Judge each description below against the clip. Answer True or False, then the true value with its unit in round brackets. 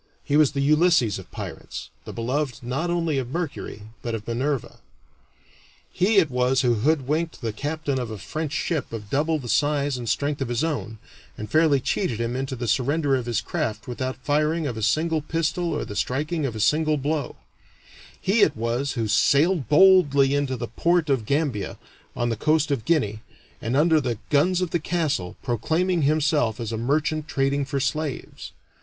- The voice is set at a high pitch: False (140 Hz)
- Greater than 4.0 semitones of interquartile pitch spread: True (4.5 semitones)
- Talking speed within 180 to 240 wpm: True (185 wpm)